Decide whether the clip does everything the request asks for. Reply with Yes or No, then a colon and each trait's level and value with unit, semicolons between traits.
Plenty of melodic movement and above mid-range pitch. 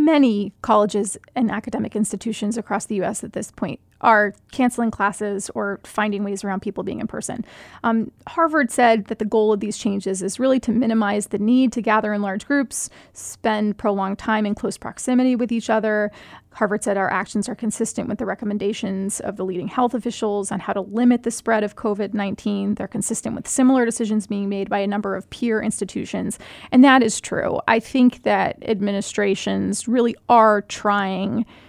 No: narrow, 2.4 semitones; high, 215 Hz